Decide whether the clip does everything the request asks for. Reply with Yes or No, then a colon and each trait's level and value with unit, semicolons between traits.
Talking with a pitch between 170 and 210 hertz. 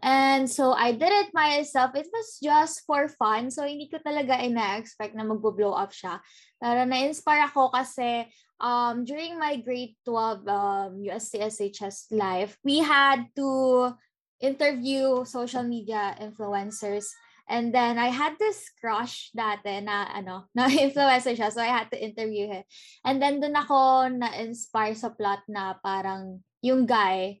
No: high, 240 Hz